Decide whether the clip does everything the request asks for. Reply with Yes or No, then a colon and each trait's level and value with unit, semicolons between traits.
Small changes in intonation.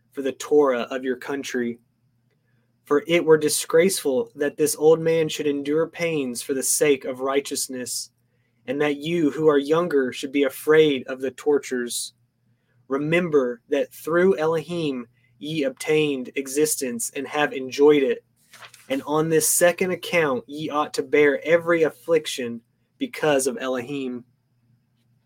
No: average, 3.7 semitones